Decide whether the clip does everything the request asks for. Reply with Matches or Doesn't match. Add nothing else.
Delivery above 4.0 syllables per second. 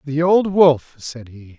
Doesn't match